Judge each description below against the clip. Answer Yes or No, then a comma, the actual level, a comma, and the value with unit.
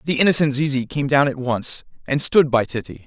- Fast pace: Yes, fast, 215 wpm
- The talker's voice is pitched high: No, low, 135 Hz